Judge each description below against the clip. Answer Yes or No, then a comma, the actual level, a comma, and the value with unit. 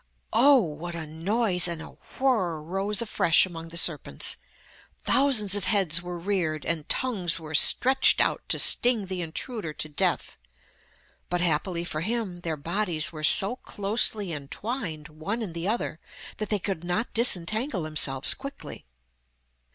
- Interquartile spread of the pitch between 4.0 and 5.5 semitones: Yes, average, 4.9 semitones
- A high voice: No, medium, 180 Hz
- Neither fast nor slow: Yes, average, 150 wpm